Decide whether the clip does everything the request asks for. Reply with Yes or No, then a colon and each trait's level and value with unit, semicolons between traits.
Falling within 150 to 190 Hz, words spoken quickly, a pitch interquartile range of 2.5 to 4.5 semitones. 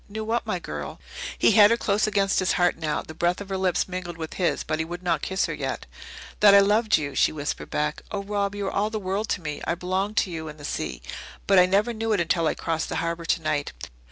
Yes: medium, 185 Hz; fast, 260 wpm; average, 3.8 semitones